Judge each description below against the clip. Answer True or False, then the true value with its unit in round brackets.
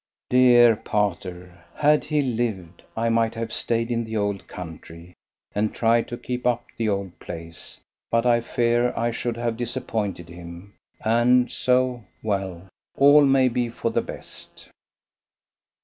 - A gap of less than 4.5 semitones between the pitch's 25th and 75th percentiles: True (3.7 semitones)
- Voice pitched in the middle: False (115 Hz)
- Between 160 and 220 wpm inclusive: False (145 wpm)